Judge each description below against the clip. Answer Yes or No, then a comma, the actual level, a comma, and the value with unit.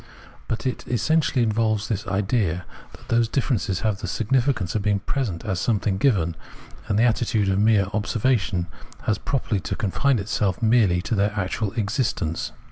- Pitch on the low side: Yes, low, 105 Hz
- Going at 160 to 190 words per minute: Yes, average, 165 wpm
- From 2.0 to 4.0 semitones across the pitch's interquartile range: Yes, average, 3.3 semitones